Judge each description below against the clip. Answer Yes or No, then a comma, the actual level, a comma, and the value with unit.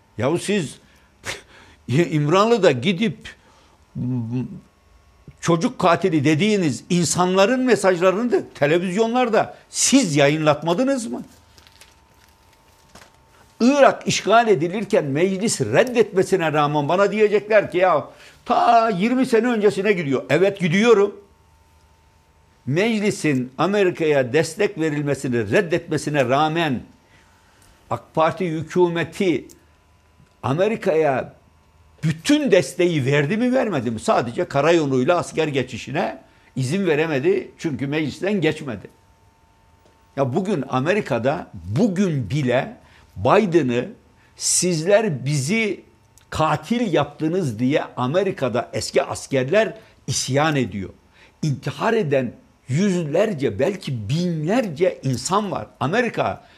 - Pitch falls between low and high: Yes, medium, 155 Hz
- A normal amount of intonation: No, wide, 8.0 semitones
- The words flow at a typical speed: No, slow, 85 wpm